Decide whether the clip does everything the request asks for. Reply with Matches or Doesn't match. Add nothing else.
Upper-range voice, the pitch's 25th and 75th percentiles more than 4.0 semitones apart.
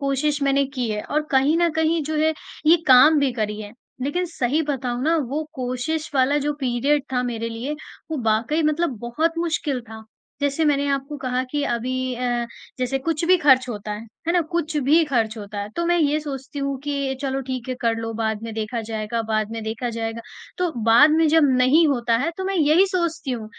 Matches